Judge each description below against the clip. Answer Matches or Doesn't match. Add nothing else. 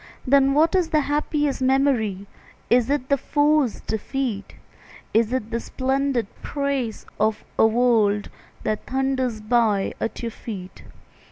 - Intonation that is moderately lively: Matches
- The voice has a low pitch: Doesn't match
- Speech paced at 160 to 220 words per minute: Doesn't match